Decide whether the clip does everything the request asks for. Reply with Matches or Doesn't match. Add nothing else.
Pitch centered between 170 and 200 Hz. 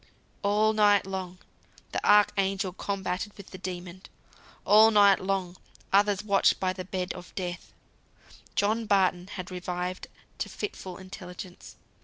Matches